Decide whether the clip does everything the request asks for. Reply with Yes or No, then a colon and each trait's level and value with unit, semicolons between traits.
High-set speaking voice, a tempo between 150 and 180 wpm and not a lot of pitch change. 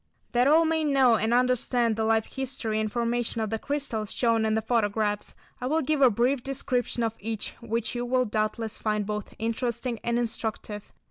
No: high, 235 Hz; average, 190 wpm; narrow, 2.3 semitones